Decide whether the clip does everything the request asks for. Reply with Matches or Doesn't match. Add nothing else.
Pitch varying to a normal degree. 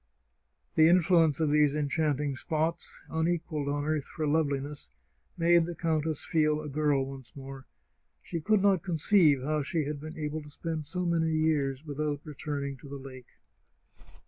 Doesn't match